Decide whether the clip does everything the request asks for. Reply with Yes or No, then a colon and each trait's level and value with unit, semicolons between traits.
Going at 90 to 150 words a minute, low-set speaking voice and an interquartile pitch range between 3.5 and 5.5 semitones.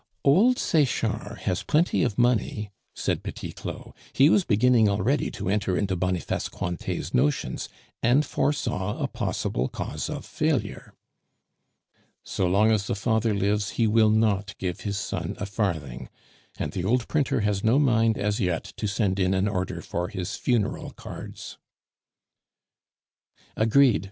Yes: average, 145 wpm; low, 105 Hz; average, 4.1 semitones